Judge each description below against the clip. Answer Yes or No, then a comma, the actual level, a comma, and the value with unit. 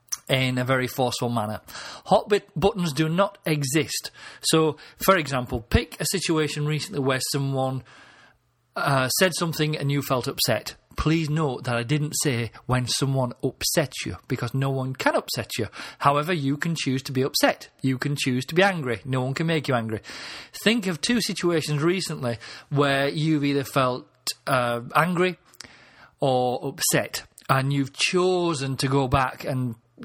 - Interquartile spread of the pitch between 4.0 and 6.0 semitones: No, average, 3.6 semitones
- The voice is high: No, medium, 140 Hz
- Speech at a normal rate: Yes, average, 165 wpm